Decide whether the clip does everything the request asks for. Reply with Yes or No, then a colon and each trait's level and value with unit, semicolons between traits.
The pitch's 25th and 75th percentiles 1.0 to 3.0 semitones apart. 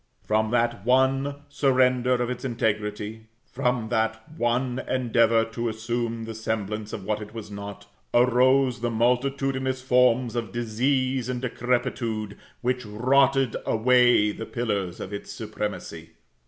Yes: narrow, 2.4 semitones